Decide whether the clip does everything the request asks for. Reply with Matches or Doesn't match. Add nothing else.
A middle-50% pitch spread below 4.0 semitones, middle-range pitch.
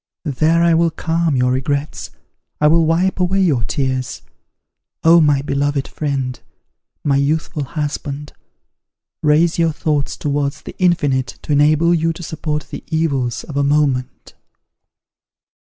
Matches